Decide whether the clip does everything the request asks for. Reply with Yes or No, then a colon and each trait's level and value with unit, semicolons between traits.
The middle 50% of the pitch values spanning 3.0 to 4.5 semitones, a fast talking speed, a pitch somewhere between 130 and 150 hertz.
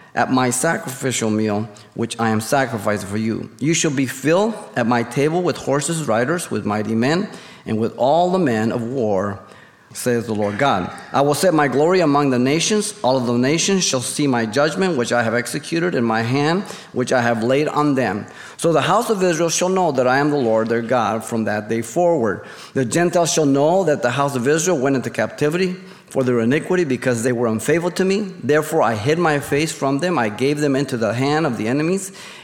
No: wide, 5.6 semitones; fast, 220 wpm; medium, 140 Hz